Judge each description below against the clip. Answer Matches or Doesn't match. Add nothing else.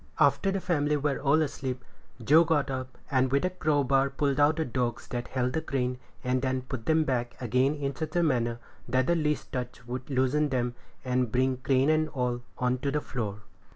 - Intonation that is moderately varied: Matches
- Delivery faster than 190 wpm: Matches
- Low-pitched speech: Matches